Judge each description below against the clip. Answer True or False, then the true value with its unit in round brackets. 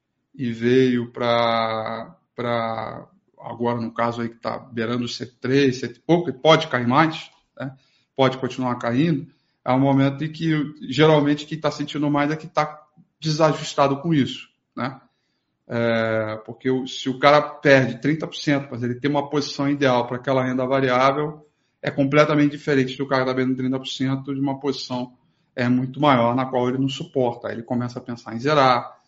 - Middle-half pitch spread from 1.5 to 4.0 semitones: True (3.2 semitones)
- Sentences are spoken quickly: False (170 wpm)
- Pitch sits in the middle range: False (130 Hz)